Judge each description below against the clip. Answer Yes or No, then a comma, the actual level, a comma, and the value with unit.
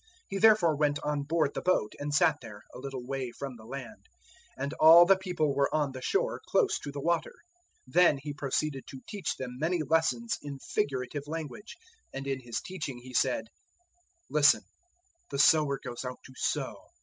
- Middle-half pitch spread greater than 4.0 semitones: No, average, 3.6 semitones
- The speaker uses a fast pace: No, average, 190 wpm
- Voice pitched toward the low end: No, medium, 145 Hz